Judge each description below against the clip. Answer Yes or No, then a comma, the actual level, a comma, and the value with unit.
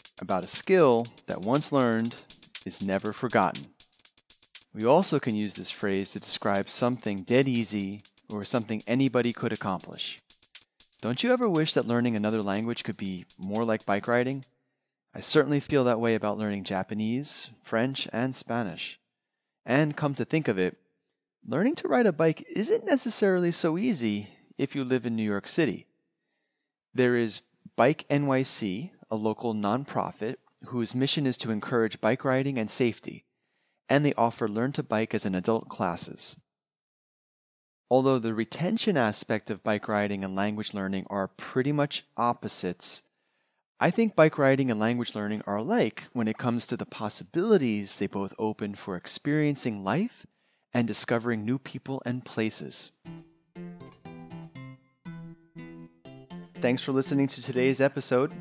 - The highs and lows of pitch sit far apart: No, average, 5.0 semitones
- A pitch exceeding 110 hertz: Yes, low, 120 Hz